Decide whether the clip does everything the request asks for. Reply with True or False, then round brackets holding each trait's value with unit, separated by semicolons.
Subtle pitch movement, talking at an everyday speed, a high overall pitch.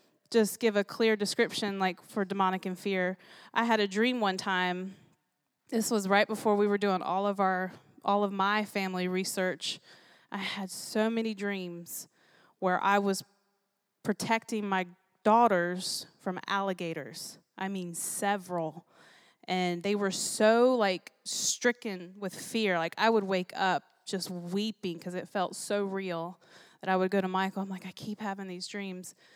True (2.2 semitones; 165 wpm; 195 Hz)